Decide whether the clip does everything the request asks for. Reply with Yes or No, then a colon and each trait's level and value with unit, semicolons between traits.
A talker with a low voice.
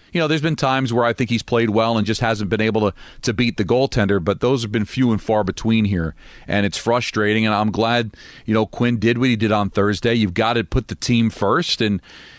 Yes: low, 115 Hz